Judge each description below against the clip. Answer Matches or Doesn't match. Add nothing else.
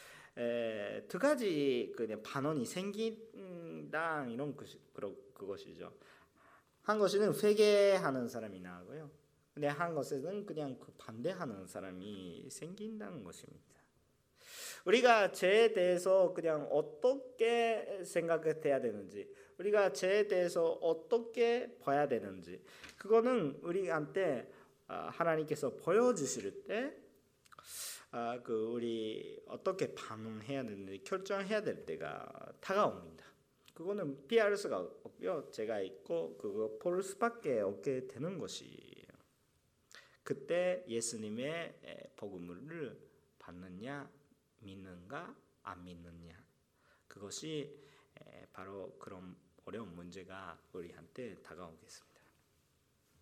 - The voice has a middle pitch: Matches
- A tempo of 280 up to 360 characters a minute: Doesn't match